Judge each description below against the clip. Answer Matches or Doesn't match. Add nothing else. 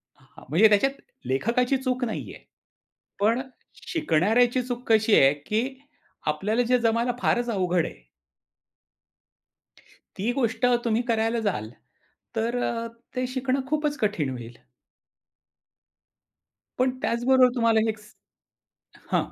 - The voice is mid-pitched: Doesn't match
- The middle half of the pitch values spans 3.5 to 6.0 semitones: Doesn't match